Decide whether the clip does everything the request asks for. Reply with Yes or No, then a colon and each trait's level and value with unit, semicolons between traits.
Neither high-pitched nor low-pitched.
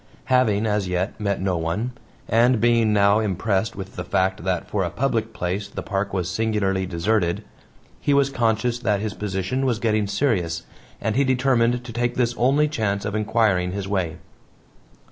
No: low, 105 Hz